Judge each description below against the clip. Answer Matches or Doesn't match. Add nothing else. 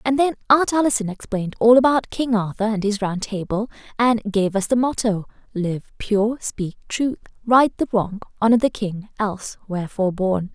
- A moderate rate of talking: Matches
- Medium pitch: Doesn't match